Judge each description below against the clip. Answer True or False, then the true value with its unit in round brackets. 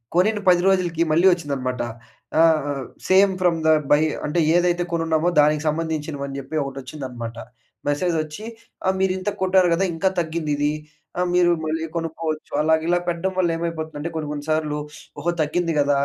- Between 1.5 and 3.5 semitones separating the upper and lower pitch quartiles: True (2.9 semitones)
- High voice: False (160 Hz)